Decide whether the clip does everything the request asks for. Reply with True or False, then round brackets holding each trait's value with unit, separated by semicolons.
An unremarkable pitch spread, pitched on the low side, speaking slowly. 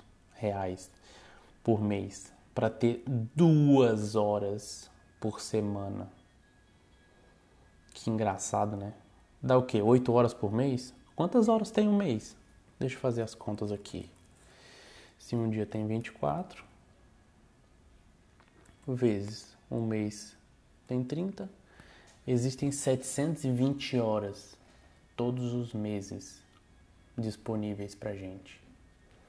True (3.9 semitones; 110 Hz; 100 wpm)